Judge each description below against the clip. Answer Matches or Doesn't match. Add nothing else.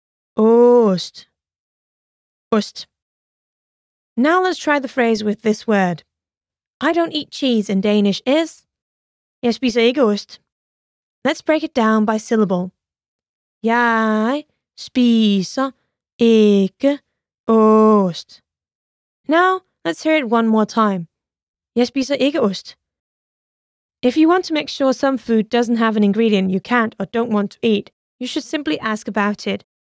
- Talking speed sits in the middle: Doesn't match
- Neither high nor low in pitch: Doesn't match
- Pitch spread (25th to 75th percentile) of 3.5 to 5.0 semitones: Matches